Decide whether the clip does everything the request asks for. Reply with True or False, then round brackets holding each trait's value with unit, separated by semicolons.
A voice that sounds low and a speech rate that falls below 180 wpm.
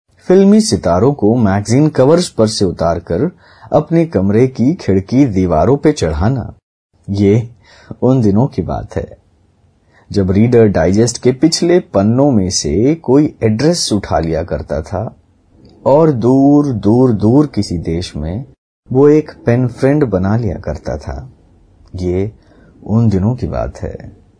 True (110 Hz; 140 wpm)